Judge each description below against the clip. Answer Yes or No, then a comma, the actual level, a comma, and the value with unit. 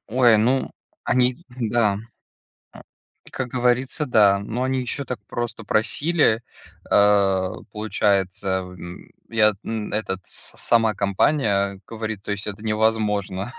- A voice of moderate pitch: No, low, 110 Hz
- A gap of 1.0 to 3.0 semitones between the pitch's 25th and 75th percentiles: No, average, 3.4 semitones